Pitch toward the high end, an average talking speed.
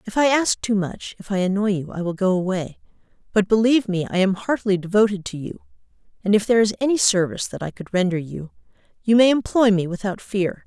No: high, 200 Hz; fast, 210 wpm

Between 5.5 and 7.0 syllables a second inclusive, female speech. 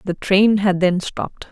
No: 4.4 syllables/s; female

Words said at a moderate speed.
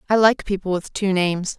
No: fast, 230 wpm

